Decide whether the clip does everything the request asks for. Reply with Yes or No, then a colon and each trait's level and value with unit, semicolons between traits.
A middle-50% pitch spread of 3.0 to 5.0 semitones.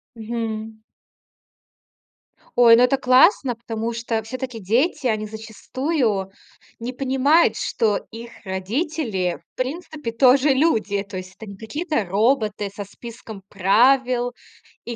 Yes: average, 3.4 semitones